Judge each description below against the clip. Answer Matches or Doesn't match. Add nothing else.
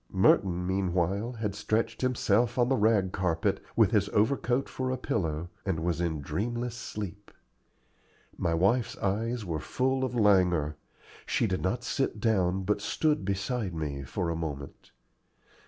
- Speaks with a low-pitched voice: Matches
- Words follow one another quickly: Doesn't match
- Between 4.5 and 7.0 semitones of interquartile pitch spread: Matches